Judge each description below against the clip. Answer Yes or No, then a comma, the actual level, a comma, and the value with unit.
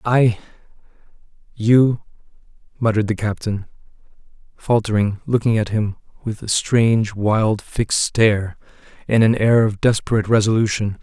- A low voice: Yes, low, 110 Hz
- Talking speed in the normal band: No, slow, 115 wpm